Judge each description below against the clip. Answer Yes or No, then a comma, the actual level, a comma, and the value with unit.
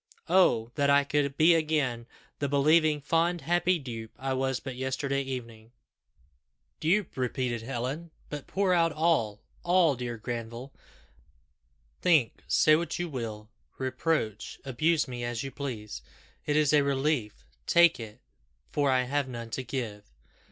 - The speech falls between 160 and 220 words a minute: No, average, 145 wpm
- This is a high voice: No, low, 135 Hz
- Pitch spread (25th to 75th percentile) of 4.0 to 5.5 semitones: Yes, average, 4.6 semitones